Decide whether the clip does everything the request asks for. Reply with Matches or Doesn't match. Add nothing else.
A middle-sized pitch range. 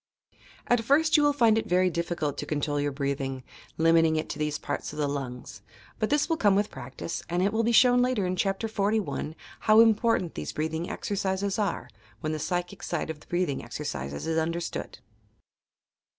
Doesn't match